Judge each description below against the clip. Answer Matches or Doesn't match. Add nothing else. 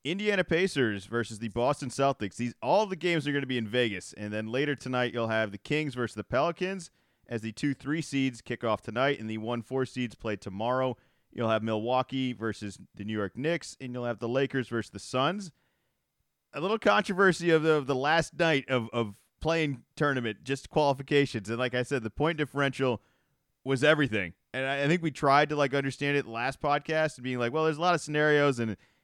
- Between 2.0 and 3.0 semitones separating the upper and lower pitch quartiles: Doesn't match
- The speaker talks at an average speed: Doesn't match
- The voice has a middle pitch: Doesn't match